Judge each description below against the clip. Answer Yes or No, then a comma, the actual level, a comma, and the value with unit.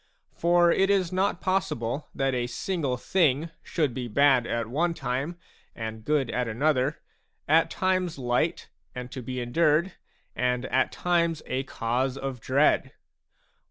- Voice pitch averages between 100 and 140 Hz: Yes, low, 135 Hz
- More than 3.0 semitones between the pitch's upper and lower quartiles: Yes, average, 5.3 semitones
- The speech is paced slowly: No, average, 145 wpm